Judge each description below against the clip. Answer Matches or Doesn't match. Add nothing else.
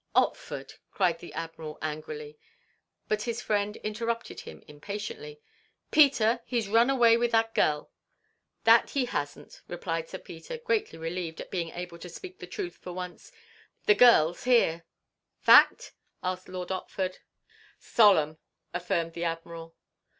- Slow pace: Doesn't match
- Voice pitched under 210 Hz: Matches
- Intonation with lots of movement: Matches